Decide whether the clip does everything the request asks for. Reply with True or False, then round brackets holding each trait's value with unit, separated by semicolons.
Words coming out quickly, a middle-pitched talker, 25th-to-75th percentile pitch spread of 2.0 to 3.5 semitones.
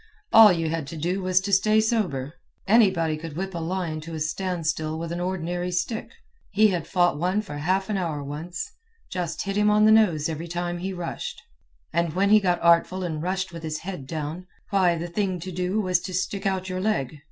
True (215 wpm; 180 Hz; 2.8 semitones)